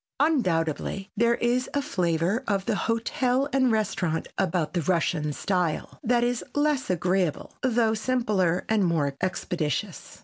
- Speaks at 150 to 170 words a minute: No, slow, 135 wpm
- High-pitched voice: Yes, high, 200 Hz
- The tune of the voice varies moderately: No, wide, 5.9 semitones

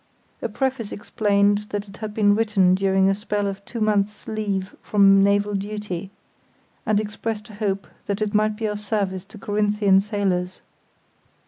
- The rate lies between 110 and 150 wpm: No, average, 160 wpm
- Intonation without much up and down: Yes, narrow, 1.3 semitones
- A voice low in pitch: No, high, 205 Hz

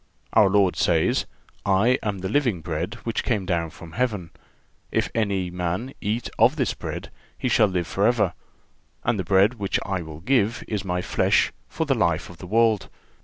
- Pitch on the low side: Yes, low, 100 Hz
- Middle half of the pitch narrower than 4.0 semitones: No, average, 4.3 semitones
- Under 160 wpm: No, average, 180 wpm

